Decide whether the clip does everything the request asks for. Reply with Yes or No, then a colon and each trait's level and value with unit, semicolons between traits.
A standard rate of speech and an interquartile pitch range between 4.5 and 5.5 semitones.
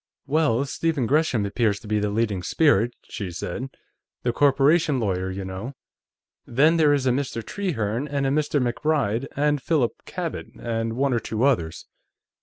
Yes: average, 165 wpm; average, 5.1 semitones